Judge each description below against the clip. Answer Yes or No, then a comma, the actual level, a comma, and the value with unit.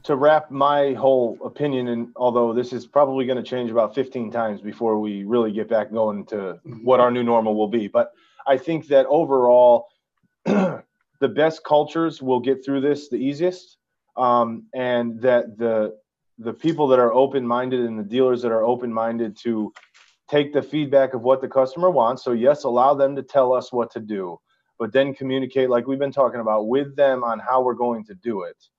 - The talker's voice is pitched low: Yes, low, 125 Hz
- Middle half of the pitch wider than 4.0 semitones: No, average, 2.8 semitones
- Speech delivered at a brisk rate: No, average, 195 wpm